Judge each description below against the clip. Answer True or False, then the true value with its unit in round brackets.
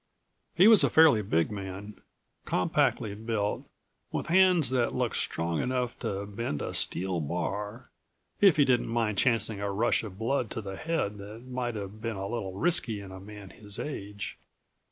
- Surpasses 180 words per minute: False (175 wpm)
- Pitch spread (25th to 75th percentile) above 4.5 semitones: False (4.0 semitones)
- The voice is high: False (105 Hz)